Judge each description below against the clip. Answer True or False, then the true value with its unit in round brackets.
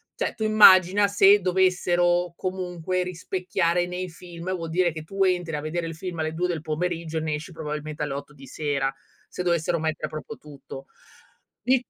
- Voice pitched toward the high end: False (175 Hz)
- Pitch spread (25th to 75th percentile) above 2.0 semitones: True (2.7 semitones)